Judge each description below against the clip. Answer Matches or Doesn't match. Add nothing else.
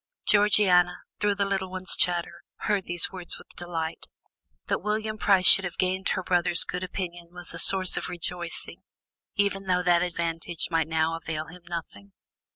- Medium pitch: Matches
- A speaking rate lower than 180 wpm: Matches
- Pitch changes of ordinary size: Doesn't match